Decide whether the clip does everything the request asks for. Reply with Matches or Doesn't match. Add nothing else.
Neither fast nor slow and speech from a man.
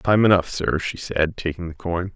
Doesn't match